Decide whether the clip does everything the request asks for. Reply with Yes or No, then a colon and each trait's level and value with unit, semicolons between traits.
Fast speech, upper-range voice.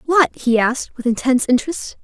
No: average, 175 wpm; very high, 265 Hz